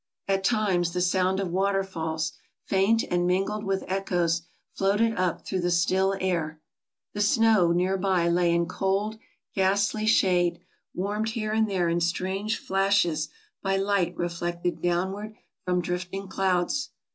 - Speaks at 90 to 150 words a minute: Yes, average, 145 wpm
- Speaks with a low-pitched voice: No, high, 190 Hz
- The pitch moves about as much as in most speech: No, narrow, 2.2 semitones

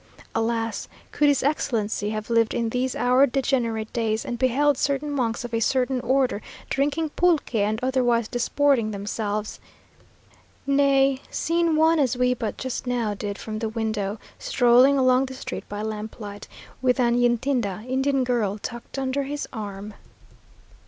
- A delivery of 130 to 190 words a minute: Yes, average, 150 wpm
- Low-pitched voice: No, high, 245 Hz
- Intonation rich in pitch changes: No, average, 3.7 semitones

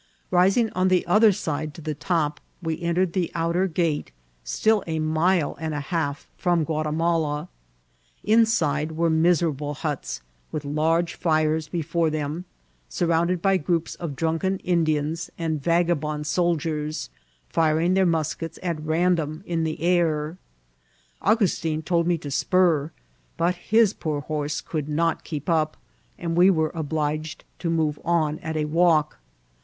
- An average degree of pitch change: No, narrow, 2.2 semitones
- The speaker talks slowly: No, average, 150 wpm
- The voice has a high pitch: No, medium, 160 Hz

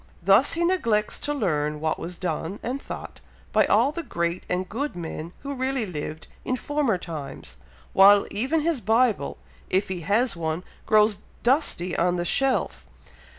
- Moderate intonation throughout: No, wide, 7.1 semitones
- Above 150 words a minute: Yes, average, 160 wpm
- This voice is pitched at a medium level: No, high, 205 Hz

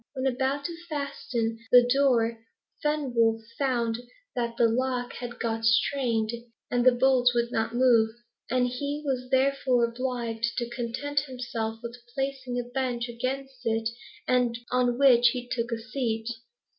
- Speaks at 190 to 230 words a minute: No, average, 145 wpm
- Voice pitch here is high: Yes, high, 245 Hz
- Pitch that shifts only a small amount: Yes, narrow, 2.0 semitones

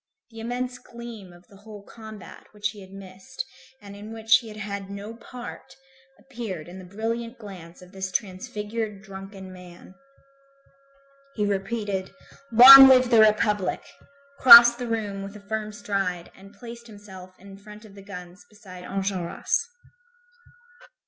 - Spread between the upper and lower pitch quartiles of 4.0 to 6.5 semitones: No, average, 2.8 semitones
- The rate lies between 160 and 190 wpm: No, average, 150 wpm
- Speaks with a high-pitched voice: Yes, high, 205 Hz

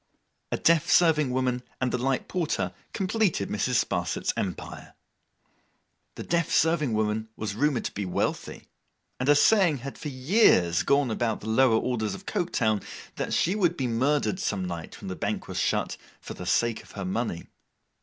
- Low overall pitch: Yes, low, 125 Hz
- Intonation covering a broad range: Yes, wide, 6.2 semitones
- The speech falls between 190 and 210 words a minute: No, average, 175 wpm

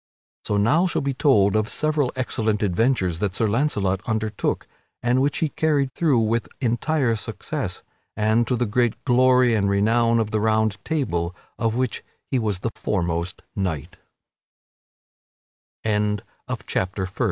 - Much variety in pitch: No, average, 3.7 semitones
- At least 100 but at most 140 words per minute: Yes, slow, 135 wpm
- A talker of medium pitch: No, low, 115 Hz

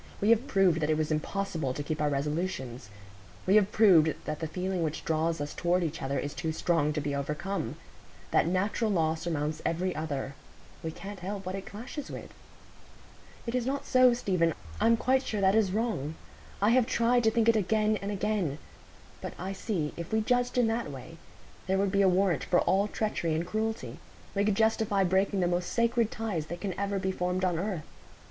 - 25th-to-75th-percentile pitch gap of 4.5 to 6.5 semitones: Yes, average, 5.0 semitones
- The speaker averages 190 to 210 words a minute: Yes, fast, 205 wpm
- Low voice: No, high, 190 Hz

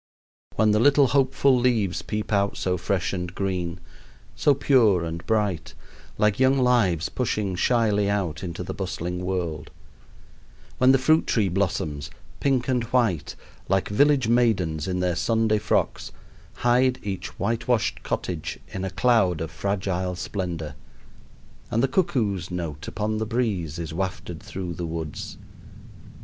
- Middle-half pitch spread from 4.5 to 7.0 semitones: Yes, average, 5.1 semitones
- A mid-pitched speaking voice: No, low, 100 Hz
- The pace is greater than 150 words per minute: No, average, 140 wpm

